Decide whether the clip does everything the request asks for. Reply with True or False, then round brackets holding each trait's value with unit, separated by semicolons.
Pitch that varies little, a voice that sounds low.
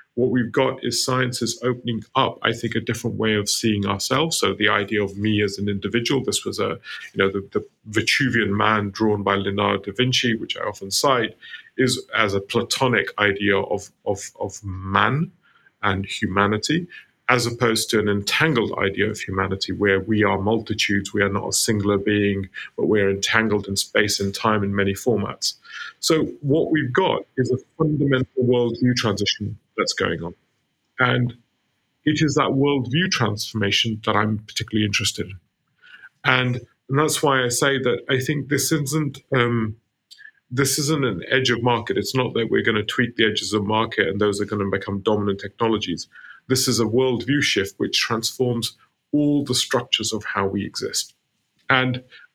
False (3.8 semitones; 110 Hz)